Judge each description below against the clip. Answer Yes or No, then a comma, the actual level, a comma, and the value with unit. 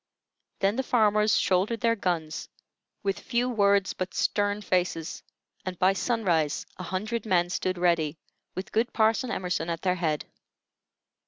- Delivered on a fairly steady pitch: No, average, 3.5 semitones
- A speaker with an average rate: Yes, average, 145 wpm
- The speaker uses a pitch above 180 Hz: Yes, high, 190 Hz